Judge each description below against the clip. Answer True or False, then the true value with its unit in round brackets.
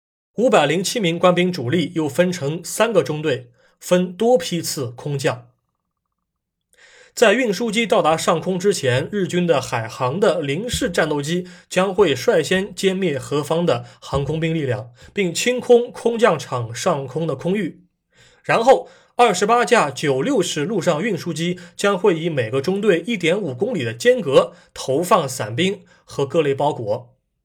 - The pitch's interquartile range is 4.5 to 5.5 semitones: True (5.2 semitones)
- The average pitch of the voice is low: False (170 Hz)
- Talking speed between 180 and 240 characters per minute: True (230 characters per minute)